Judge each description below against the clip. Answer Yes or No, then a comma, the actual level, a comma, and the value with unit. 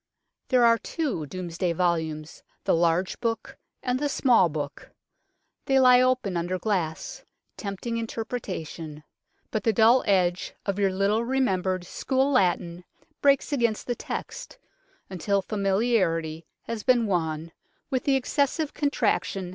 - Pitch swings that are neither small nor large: No, wide, 6.1 semitones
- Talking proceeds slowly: Yes, slow, 130 wpm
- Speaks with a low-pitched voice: No, high, 200 Hz